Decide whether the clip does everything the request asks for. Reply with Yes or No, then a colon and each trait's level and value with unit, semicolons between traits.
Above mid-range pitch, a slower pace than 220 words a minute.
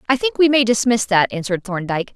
No: high, 220 Hz; fast, 225 wpm